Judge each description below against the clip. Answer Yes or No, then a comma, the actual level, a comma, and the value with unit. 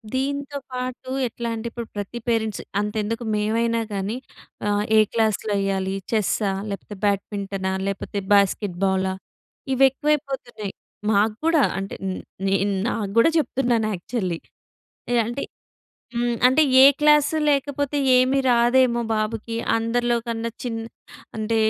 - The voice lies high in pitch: Yes, high, 230 Hz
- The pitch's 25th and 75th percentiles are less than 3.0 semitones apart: No, average, 3.7 semitones